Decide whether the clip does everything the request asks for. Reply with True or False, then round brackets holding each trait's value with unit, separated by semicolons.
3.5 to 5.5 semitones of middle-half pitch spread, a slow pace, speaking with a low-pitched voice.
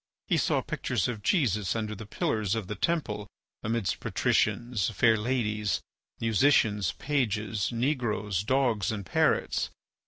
False (2.9 semitones; 125 wpm; 110 Hz)